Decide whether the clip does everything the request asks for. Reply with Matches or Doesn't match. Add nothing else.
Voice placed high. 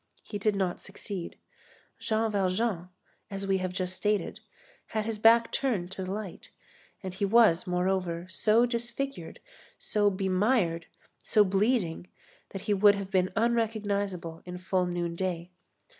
Matches